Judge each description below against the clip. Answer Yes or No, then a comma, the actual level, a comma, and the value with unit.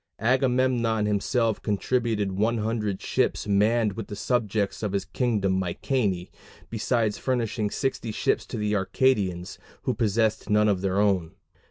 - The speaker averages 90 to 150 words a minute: Yes, slow, 135 wpm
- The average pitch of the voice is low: Yes, low, 105 Hz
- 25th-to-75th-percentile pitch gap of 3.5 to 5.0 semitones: No, average, 2.8 semitones